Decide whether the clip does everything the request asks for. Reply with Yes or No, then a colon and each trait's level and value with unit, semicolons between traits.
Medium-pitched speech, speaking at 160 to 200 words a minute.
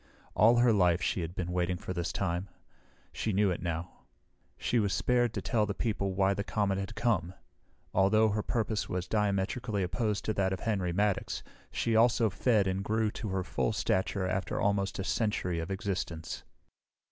No: low, 100 Hz; average, 180 wpm